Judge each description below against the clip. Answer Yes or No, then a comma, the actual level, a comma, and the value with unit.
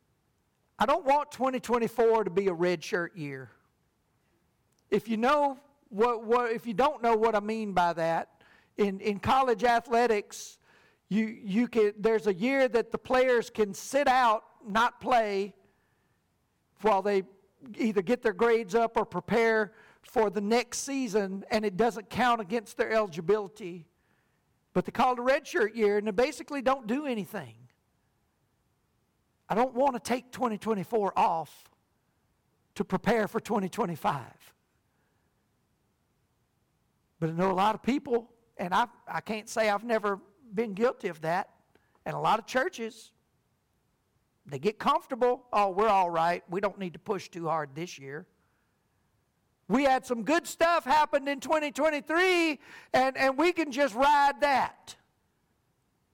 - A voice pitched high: Yes, high, 225 Hz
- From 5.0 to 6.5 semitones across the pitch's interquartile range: No, average, 4.0 semitones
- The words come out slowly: No, average, 150 wpm